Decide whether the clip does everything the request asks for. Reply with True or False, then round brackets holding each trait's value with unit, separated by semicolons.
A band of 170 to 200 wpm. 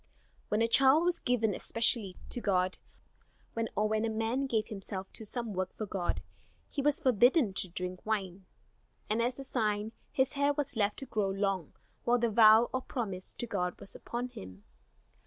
True (180 wpm)